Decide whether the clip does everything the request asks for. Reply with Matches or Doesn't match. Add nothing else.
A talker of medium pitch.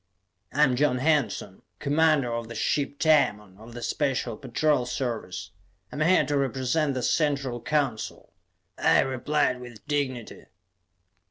Doesn't match